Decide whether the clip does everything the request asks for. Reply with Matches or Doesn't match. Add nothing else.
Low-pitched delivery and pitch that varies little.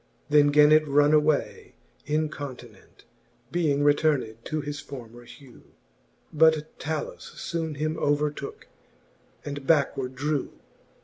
Doesn't match